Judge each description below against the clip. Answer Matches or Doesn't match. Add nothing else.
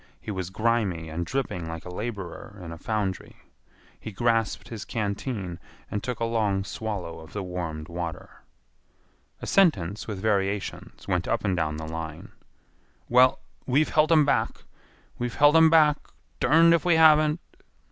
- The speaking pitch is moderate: Doesn't match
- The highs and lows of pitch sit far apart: Matches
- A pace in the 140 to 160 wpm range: Matches